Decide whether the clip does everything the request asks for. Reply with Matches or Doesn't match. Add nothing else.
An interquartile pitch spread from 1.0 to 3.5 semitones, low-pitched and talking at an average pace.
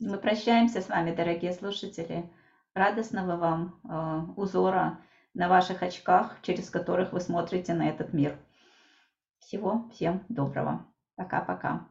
Doesn't match